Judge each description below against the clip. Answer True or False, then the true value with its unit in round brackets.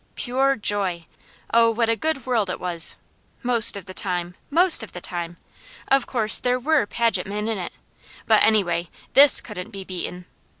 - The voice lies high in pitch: True (215 Hz)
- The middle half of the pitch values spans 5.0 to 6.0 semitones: True (5.3 semitones)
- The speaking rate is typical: True (175 wpm)